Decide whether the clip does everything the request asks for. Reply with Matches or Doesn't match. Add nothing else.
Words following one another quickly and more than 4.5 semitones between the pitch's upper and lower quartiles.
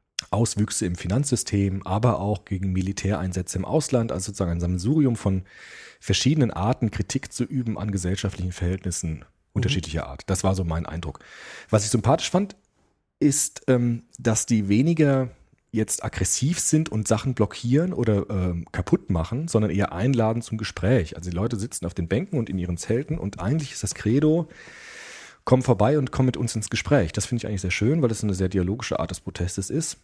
Doesn't match